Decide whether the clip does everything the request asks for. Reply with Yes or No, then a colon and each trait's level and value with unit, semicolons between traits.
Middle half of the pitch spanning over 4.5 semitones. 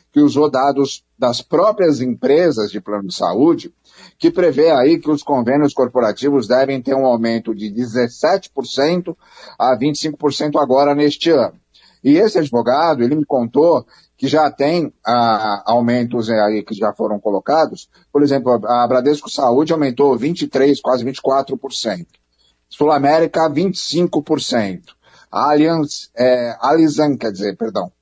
No: average, 3.9 semitones